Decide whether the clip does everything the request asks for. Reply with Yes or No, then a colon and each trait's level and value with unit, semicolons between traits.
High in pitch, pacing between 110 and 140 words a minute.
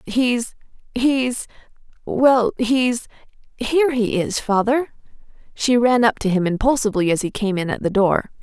Yes: high, 230 Hz; slow, 135 wpm